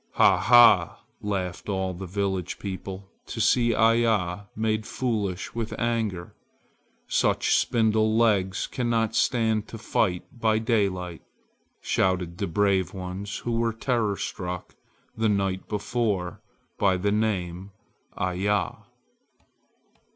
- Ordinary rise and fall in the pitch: Yes, average, 3.3 semitones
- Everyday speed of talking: No, slow, 115 wpm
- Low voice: Yes, low, 105 Hz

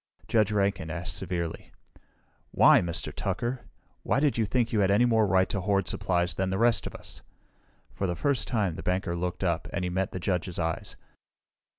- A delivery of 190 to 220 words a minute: Yes, average, 195 wpm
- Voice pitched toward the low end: Yes, very low, 95 Hz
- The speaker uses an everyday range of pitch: Yes, average, 3.6 semitones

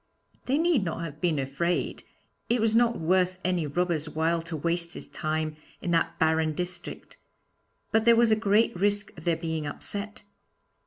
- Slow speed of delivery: No, average, 170 wpm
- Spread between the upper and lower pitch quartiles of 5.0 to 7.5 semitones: No, average, 4.3 semitones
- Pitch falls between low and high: Yes, medium, 175 Hz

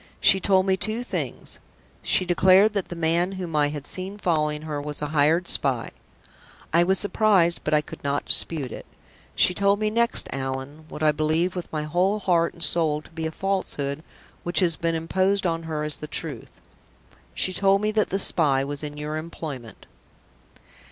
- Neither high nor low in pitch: Yes, medium, 165 Hz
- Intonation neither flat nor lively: Yes, average, 3.9 semitones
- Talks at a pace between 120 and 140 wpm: No, average, 190 wpm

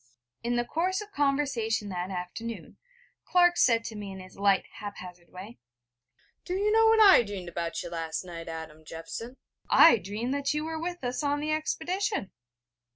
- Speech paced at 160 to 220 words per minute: Yes, average, 180 wpm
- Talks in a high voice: Yes, high, 230 Hz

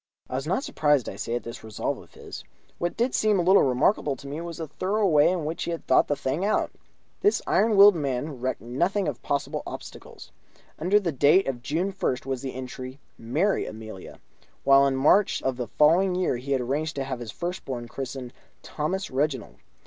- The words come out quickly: Yes, fast, 210 wpm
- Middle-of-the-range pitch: Yes, medium, 145 Hz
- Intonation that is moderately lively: No, wide, 5.7 semitones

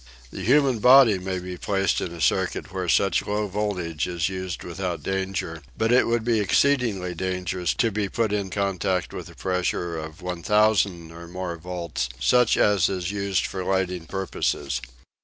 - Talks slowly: No, average, 170 wpm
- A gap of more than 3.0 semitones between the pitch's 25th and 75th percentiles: No, average, 2.7 semitones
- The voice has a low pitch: Yes, very low, 95 Hz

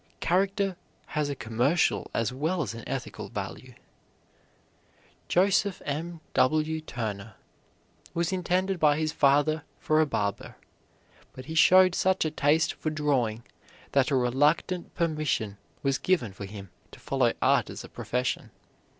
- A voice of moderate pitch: Yes, medium, 155 Hz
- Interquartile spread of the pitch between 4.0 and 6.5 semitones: Yes, average, 5.2 semitones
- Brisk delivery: No, average, 140 wpm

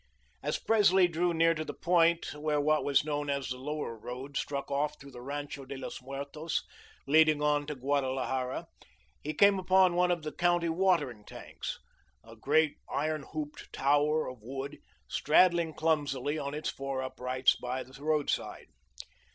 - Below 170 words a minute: Yes, average, 160 wpm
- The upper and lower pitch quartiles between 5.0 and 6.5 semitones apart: No, average, 2.7 semitones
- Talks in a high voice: No, medium, 145 Hz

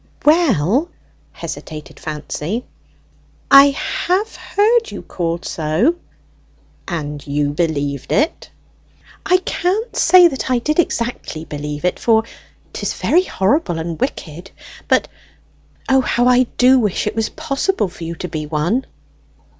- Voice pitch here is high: Yes, high, 215 Hz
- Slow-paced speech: Yes, slow, 130 wpm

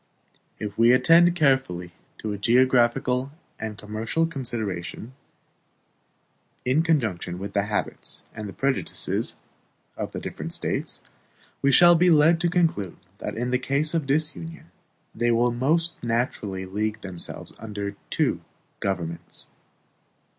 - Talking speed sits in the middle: No, slow, 120 wpm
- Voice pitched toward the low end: Yes, low, 120 Hz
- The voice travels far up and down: Yes, wide, 6.6 semitones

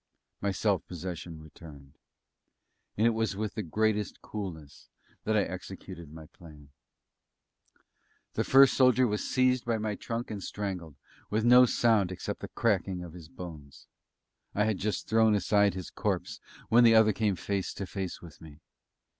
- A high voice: No, low, 100 Hz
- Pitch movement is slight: No, average, 4.3 semitones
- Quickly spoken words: No, average, 160 wpm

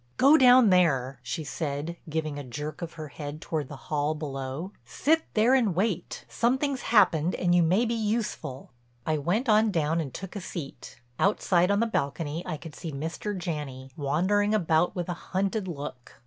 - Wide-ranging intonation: Yes, wide, 5.8 semitones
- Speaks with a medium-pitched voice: Yes, medium, 170 Hz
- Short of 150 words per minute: No, average, 180 wpm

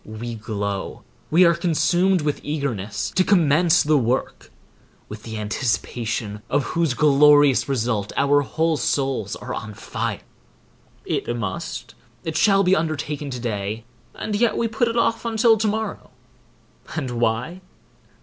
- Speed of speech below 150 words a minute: Yes, average, 140 wpm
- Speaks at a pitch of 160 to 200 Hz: No, medium, 145 Hz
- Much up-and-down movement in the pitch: Yes, wide, 6.8 semitones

